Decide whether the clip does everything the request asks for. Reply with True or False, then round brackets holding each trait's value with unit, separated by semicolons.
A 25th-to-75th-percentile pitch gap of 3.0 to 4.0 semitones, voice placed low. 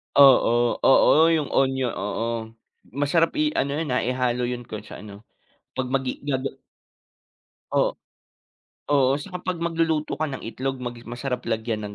True (3.3 semitones; 130 Hz)